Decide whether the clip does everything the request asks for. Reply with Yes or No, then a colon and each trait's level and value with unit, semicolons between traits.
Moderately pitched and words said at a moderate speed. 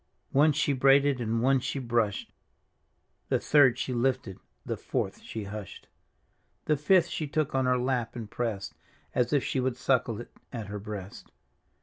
No: low, 125 Hz; average, 165 wpm